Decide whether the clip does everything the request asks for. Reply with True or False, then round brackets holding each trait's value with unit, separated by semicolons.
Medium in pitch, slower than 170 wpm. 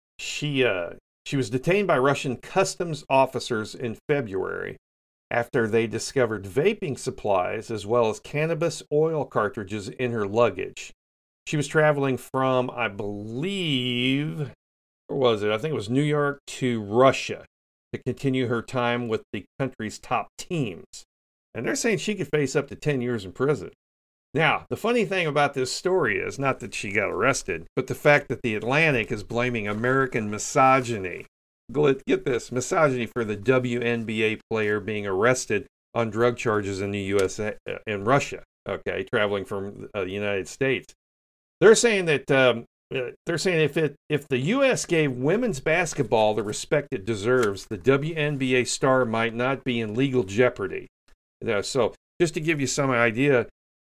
False (125 Hz; 160 wpm)